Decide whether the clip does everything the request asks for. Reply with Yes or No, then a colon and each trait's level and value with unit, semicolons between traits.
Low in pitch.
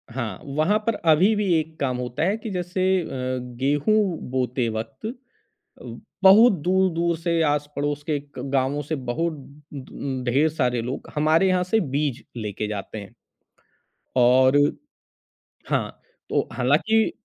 No: medium, 150 Hz